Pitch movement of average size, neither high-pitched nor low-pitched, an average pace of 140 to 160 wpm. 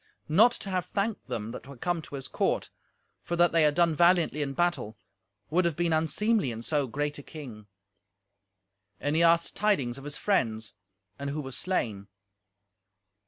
No: average, 4.4 semitones; medium, 155 Hz; average, 175 wpm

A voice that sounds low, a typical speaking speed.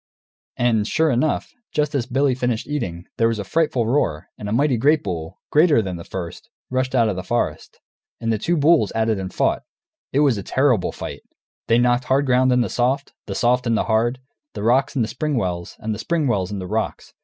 No: low, 120 Hz; fast, 215 wpm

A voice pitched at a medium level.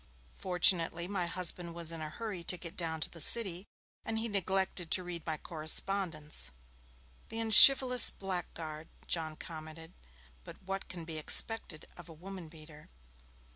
Yes: medium, 170 Hz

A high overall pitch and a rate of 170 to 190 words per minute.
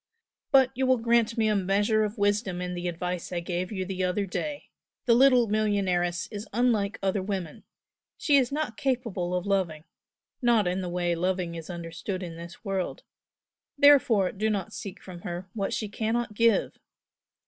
Yes: high, 200 Hz; average, 175 wpm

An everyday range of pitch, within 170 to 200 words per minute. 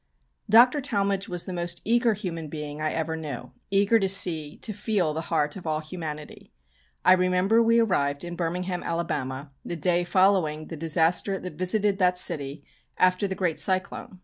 Yes: average, 3.9 semitones; average, 175 wpm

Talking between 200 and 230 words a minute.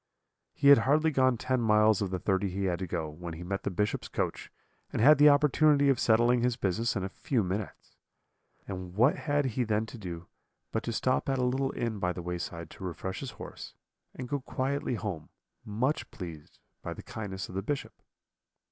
Yes: fast, 205 wpm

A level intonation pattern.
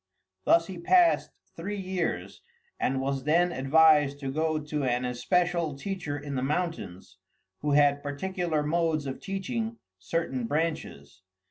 No: average, 4.1 semitones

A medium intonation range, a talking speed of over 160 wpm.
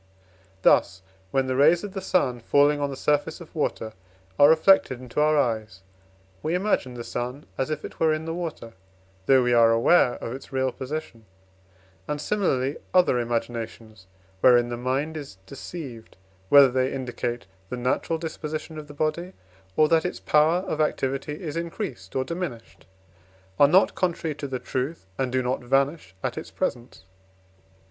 Yes: average, 4.3 semitones; average, 170 wpm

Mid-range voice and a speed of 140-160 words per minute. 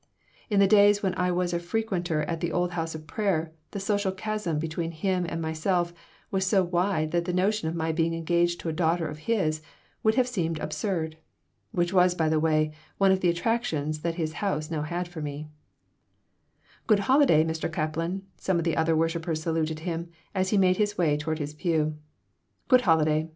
No: medium, 170 Hz; average, 200 wpm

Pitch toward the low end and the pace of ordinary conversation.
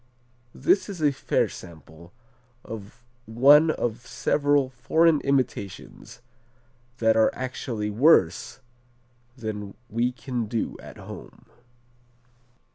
No: low, 120 Hz; slow, 100 wpm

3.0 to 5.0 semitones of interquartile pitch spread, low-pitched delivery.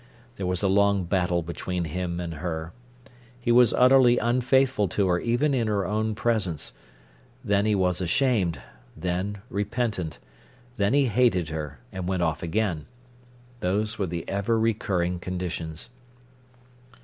Yes: average, 4.2 semitones; very low, 95 Hz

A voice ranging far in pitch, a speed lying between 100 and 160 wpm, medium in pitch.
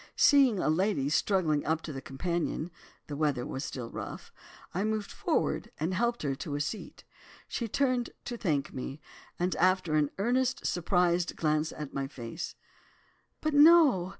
Yes: wide, 6.5 semitones; average, 150 wpm; medium, 175 Hz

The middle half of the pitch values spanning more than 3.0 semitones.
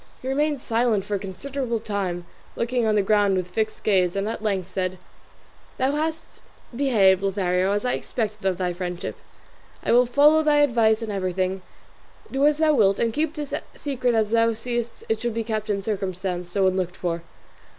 Yes: average, 4.6 semitones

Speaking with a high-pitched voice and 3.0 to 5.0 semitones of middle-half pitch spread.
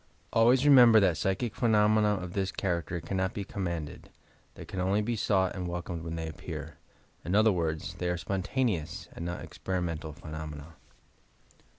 No: very low, 90 Hz; average, 4.1 semitones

